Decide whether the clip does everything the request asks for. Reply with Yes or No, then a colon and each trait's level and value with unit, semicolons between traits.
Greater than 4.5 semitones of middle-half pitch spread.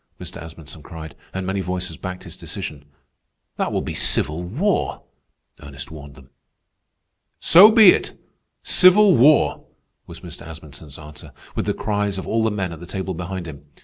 Yes: average, 5.0 semitones